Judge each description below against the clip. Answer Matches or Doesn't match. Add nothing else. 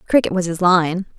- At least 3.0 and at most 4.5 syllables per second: Doesn't match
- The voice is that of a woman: Matches